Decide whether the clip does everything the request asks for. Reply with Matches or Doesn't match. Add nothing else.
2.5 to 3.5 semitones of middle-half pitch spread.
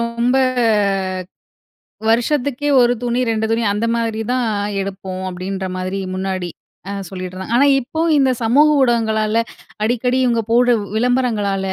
Doesn't match